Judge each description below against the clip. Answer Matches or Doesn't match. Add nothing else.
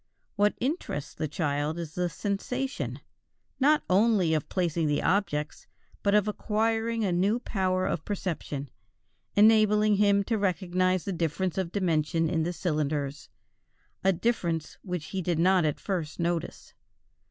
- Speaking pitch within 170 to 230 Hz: Matches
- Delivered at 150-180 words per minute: Doesn't match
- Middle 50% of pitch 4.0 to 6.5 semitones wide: Matches